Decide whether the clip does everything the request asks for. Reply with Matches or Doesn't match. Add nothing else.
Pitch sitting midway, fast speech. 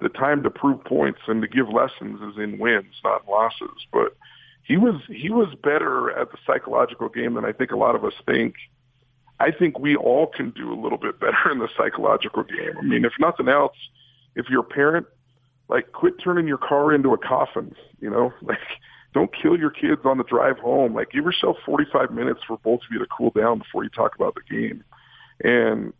Matches